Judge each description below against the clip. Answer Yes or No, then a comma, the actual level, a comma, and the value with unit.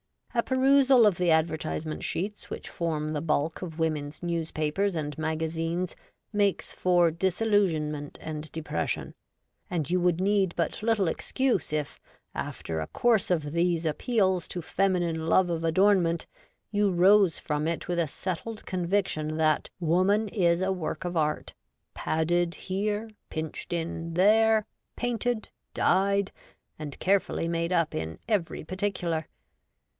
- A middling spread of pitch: Yes, average, 3.8 semitones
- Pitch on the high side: No, medium, 175 Hz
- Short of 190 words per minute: Yes, average, 140 wpm